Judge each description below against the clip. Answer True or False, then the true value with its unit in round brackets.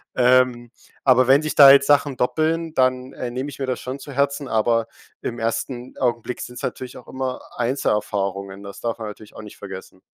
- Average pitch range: True (3.0 semitones)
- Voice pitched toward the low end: True (125 Hz)